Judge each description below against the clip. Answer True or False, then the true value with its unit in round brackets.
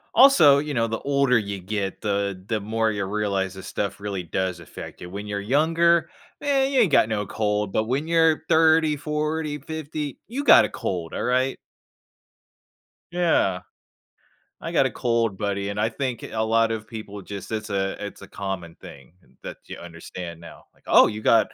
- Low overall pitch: True (110 Hz)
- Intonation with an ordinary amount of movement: False (6.9 semitones)